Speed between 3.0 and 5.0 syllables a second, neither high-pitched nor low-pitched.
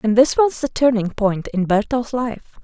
No: 4.4 syllables/s; high, 230 Hz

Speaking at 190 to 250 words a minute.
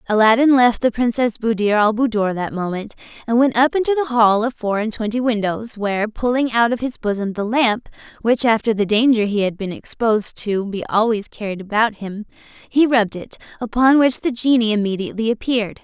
Yes: average, 195 wpm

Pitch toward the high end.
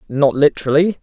No: medium, 150 Hz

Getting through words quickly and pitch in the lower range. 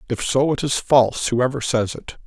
Yes: fast, 210 wpm; low, 130 Hz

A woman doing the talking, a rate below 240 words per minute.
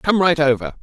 No: male; fast, 220 wpm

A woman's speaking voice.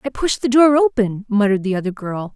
Yes: female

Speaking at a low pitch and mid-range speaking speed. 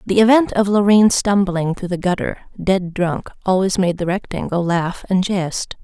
No: high, 190 Hz; average, 175 wpm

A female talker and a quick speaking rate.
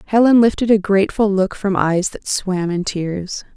No: female; average, 185 wpm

